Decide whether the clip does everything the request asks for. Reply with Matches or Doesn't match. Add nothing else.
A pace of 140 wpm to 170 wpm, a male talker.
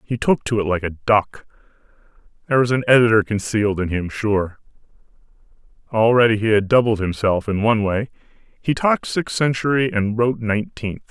Matches